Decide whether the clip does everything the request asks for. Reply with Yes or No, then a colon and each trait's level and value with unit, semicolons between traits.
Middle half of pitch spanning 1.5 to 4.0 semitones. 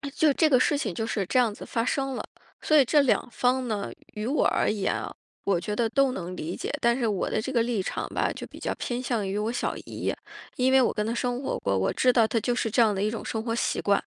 Yes: average, 3.4 semitones